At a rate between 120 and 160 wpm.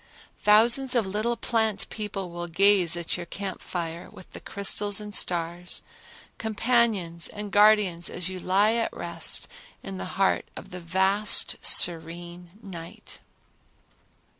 Yes: average, 140 wpm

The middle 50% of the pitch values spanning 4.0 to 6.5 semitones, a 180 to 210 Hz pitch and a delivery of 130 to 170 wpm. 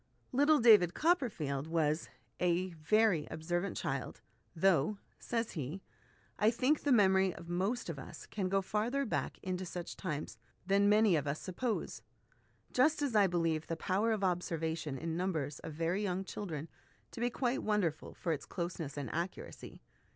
Yes: average, 4.7 semitones; medium, 185 Hz; average, 165 wpm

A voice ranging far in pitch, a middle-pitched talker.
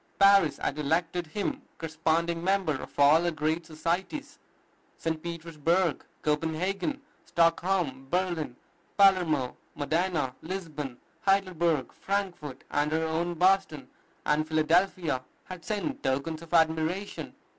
No: average, 3.1 semitones; medium, 165 Hz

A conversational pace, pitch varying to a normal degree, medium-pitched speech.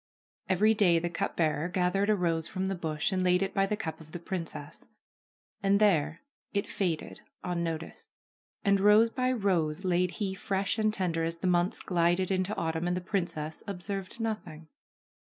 Yes: average, 175 wpm; average, 3.0 semitones; medium, 180 Hz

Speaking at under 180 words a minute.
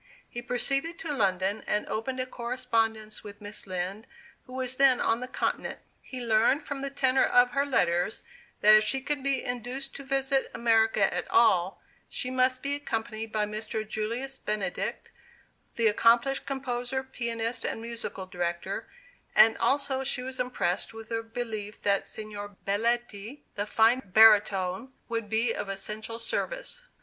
Yes: average, 155 wpm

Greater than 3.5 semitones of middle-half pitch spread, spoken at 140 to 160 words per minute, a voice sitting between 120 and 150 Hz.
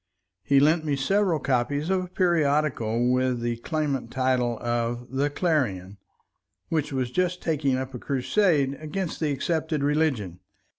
Yes: average, 4.2 semitones; average, 145 wpm; medium, 140 Hz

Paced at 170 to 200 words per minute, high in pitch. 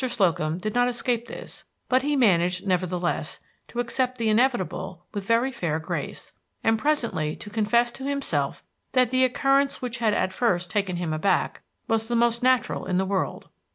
Yes: average, 175 wpm; high, 225 Hz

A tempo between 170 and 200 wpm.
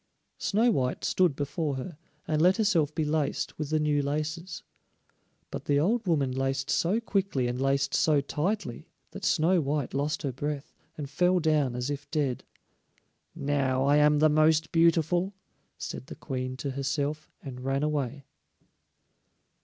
No: average, 155 wpm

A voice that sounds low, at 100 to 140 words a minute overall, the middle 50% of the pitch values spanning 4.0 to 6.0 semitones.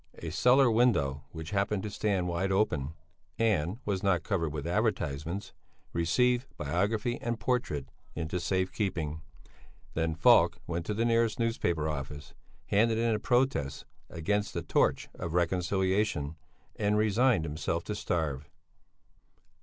Yes: very low, 95 Hz; slow, 135 wpm; average, 5.2 semitones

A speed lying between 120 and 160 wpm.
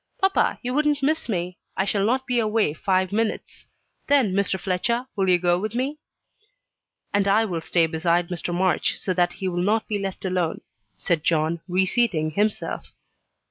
No: average, 175 wpm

